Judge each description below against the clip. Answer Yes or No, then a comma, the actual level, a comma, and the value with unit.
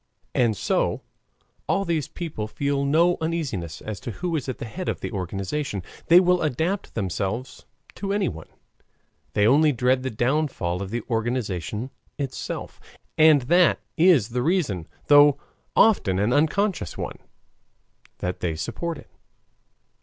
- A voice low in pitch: Yes, low, 130 Hz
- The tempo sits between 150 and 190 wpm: No, average, 140 wpm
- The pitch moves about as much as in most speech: No, wide, 7.2 semitones